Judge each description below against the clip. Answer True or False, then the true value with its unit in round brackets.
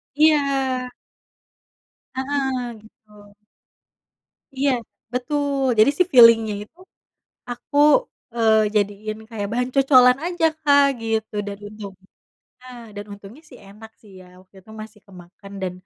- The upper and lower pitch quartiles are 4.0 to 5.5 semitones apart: True (4.4 semitones)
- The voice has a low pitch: False (230 Hz)